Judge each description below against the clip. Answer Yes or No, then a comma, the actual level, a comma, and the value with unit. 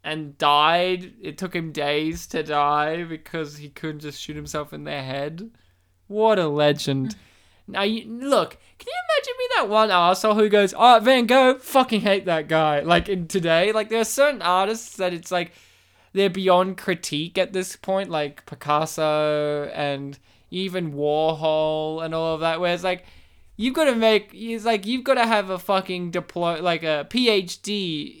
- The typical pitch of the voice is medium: Yes, medium, 175 Hz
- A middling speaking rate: Yes, average, 175 wpm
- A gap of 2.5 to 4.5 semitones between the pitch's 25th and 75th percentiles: No, wide, 5.6 semitones